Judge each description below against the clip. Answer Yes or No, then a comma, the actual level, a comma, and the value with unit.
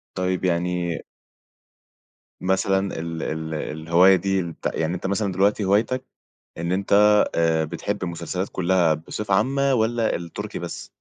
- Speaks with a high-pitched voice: No, very low, 95 Hz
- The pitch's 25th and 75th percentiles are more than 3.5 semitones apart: No, average, 2.9 semitones